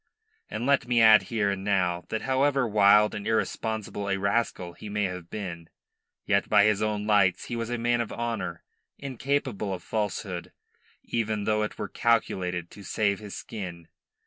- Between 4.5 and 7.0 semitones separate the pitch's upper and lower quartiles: No, average, 3.0 semitones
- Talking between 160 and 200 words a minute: Yes, average, 170 wpm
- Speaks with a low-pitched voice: Yes, low, 105 Hz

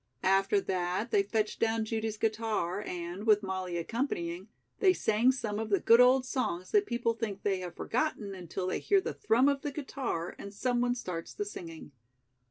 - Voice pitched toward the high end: Yes, high, 215 Hz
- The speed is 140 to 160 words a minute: No, average, 180 wpm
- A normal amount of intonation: Yes, average, 4.6 semitones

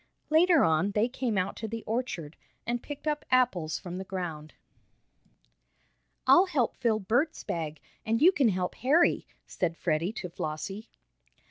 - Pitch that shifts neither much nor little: No, wide, 6.6 semitones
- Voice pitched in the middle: No, high, 215 Hz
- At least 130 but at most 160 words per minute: Yes, average, 150 wpm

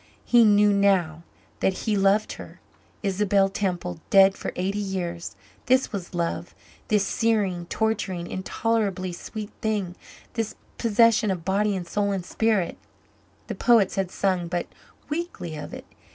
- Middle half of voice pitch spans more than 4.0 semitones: No, average, 2.9 semitones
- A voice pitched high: Yes, high, 195 Hz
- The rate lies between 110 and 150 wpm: Yes, average, 140 wpm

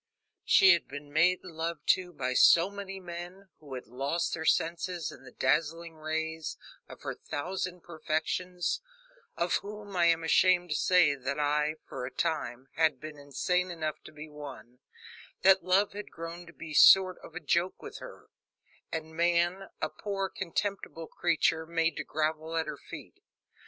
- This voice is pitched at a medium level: Yes, medium, 165 Hz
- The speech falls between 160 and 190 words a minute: Yes, average, 165 wpm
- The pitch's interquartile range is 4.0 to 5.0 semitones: No, average, 2.8 semitones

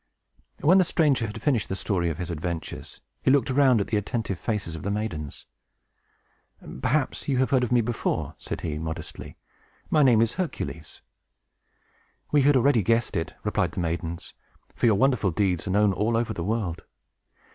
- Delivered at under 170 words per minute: No, average, 180 wpm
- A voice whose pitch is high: No, low, 110 Hz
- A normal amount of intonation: No, wide, 6.5 semitones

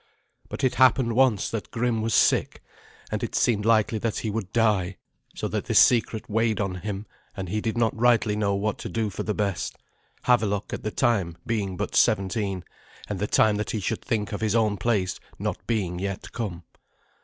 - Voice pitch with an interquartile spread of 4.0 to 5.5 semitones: No, narrow, 2.4 semitones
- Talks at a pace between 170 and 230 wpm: Yes, average, 200 wpm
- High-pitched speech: No, low, 105 Hz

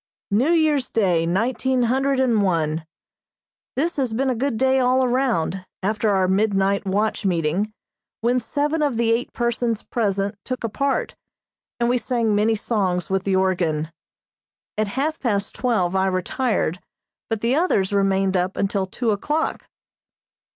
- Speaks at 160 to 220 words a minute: No, average, 150 wpm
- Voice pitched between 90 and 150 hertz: No, high, 220 Hz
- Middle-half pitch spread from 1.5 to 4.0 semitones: No, average, 4.9 semitones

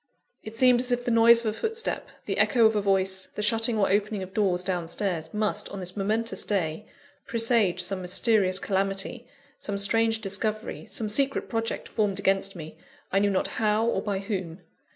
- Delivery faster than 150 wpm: Yes, average, 190 wpm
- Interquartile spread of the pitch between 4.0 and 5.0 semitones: No, average, 2.9 semitones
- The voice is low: No, high, 210 Hz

